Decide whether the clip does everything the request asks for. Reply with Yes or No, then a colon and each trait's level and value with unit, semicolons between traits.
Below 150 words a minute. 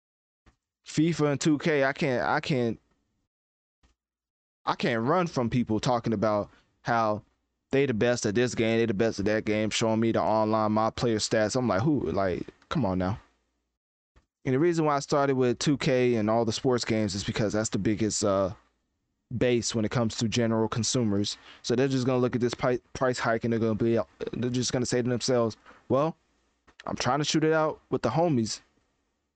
No: average, 200 wpm